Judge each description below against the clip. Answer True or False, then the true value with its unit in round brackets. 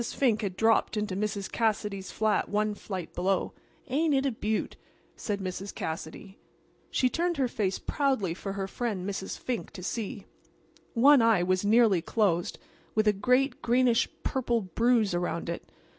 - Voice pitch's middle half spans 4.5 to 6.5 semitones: False (3.9 semitones)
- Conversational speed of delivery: True (160 wpm)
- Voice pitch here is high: True (210 Hz)